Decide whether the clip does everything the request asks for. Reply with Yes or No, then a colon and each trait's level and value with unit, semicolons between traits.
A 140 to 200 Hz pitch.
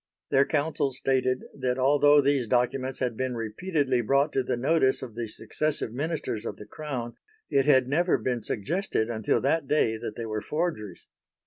No: low, 130 Hz